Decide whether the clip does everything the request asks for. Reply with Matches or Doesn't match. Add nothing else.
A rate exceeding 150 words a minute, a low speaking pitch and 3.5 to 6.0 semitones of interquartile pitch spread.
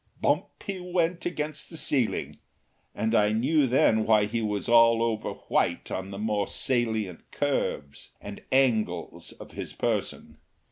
Doesn't match